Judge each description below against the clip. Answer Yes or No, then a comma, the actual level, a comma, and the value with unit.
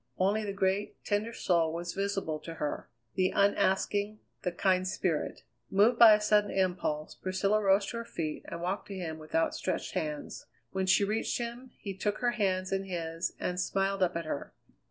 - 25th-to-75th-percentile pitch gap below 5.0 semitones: Yes, average, 2.9 semitones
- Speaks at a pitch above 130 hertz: Yes, high, 190 Hz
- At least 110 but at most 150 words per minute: No, average, 185 wpm